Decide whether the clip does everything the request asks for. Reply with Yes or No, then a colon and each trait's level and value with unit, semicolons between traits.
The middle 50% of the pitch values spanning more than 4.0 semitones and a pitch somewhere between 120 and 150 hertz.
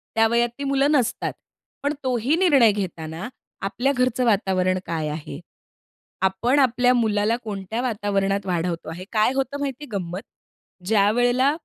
No: average, 4.9 semitones; high, 220 Hz